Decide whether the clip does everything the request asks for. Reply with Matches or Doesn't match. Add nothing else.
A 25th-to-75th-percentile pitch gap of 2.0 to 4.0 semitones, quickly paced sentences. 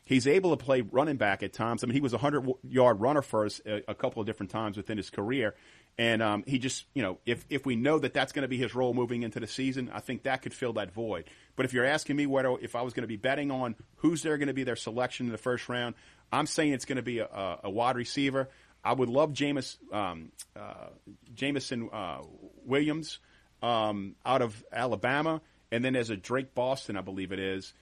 Matches